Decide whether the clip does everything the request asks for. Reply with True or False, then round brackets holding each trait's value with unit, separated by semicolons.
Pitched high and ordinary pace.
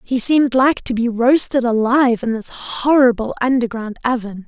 True (245 Hz; 160 wpm)